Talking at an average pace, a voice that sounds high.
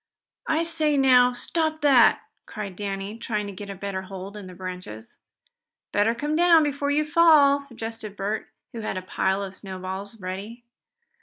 Yes: average, 165 wpm; high, 215 Hz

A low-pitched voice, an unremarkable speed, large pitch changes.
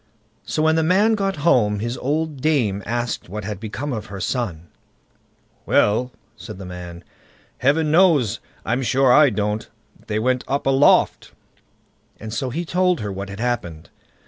Yes: low, 120 Hz; average, 160 wpm; wide, 6.2 semitones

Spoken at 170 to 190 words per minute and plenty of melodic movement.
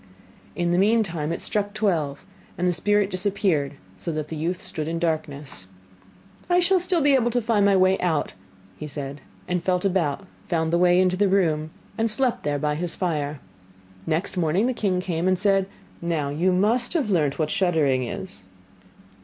No: average, 185 wpm; average, 4.4 semitones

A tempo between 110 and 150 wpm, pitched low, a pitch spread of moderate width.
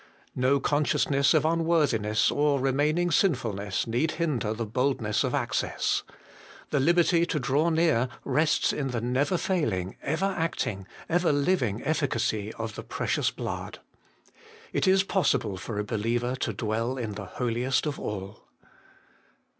No: average, 140 wpm; low, 130 Hz; wide, 6.0 semitones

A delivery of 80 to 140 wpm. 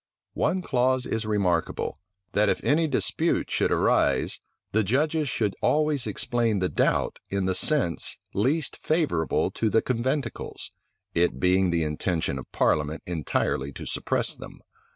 Yes: slow, 135 wpm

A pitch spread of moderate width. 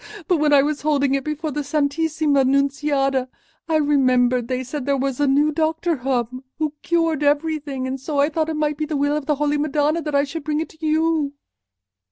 No: narrow, 2.1 semitones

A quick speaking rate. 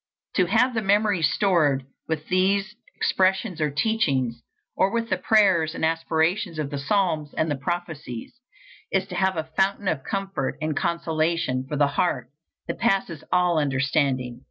No: average, 155 wpm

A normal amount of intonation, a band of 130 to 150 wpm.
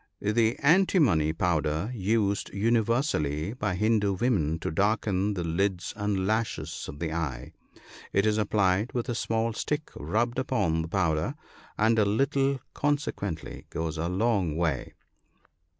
No: wide, 5.7 semitones; slow, 135 wpm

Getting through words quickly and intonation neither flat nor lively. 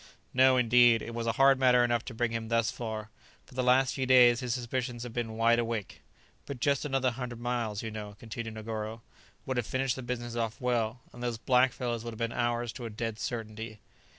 No: fast, 220 wpm; narrow, 1.7 semitones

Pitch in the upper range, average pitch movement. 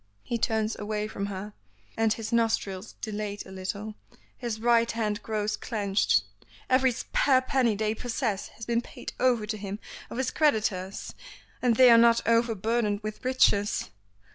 No: high, 220 Hz; narrow, 2.2 semitones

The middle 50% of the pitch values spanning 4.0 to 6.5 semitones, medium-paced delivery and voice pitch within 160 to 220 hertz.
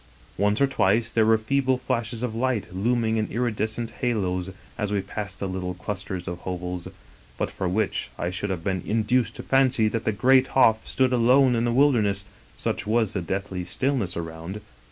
No: average, 4.3 semitones; average, 180 wpm; low, 110 Hz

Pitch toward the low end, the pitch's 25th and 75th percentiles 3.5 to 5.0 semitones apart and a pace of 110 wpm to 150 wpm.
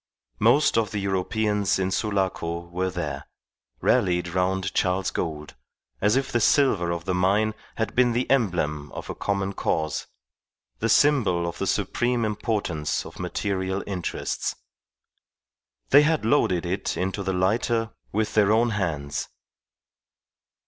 Yes: very low, 95 Hz; average, 3.9 semitones; slow, 135 wpm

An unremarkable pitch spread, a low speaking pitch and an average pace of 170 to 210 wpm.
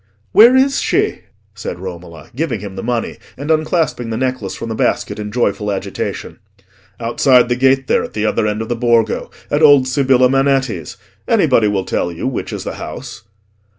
Yes: average, 4.2 semitones; low, 120 Hz; average, 185 wpm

